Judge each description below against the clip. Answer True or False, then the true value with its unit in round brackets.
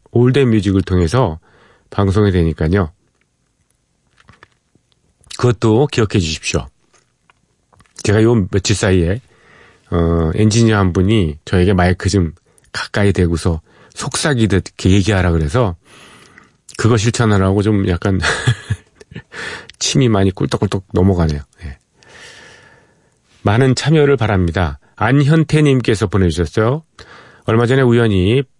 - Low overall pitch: True (100 Hz)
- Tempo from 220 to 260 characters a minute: True (245 characters per minute)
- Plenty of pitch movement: False (4.5 semitones)